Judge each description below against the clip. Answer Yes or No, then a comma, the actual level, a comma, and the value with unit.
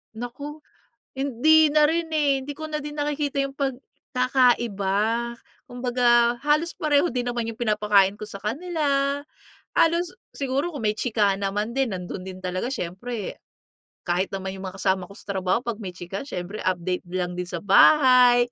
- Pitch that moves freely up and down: Yes, wide, 6.3 semitones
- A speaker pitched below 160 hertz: No, high, 240 Hz